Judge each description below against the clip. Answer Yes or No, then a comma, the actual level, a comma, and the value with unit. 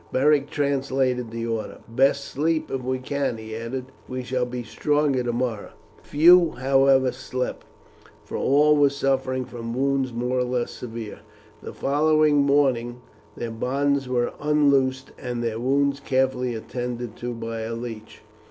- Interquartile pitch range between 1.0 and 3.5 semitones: Yes, narrow, 2.6 semitones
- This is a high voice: No, low, 130 Hz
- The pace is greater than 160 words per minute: No, average, 145 wpm